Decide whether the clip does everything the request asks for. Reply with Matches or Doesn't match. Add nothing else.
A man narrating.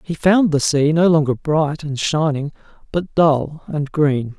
Matches